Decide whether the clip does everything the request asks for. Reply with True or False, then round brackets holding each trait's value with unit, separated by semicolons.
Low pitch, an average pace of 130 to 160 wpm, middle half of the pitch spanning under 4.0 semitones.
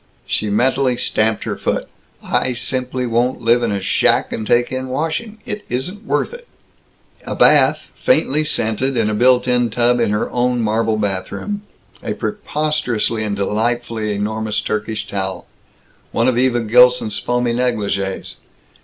True (120 Hz; 150 wpm; 3.0 semitones)